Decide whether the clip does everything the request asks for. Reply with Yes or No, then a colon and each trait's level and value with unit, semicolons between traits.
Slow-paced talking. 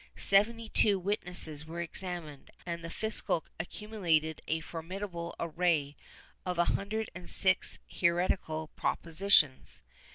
Yes: slow, 120 wpm